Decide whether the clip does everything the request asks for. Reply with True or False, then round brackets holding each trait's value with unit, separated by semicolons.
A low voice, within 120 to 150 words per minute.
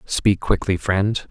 True (95 Hz; 140 wpm)